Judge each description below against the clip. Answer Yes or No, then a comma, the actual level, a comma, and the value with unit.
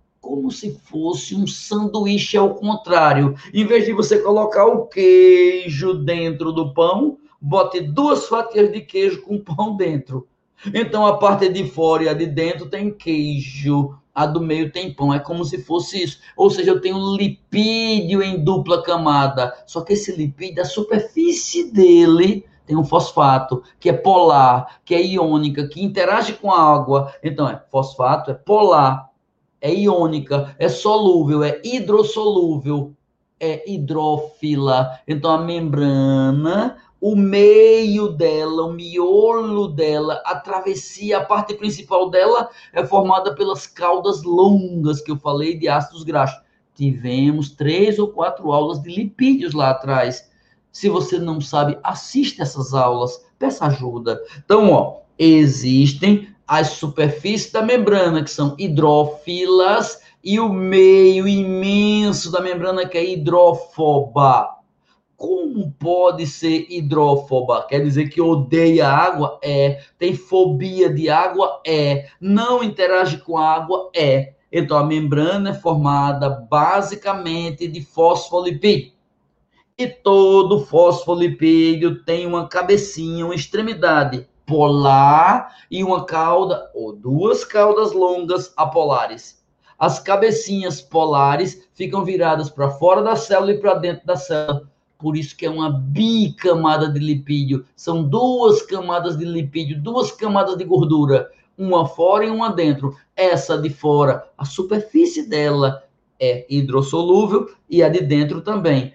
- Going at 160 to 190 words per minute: No, average, 135 wpm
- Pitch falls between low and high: Yes, medium, 170 Hz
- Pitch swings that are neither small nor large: Yes, average, 5.0 semitones